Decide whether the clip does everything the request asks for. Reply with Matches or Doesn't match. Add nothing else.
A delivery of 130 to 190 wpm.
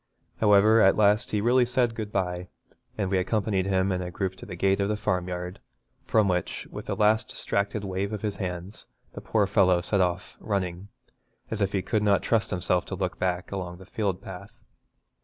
Doesn't match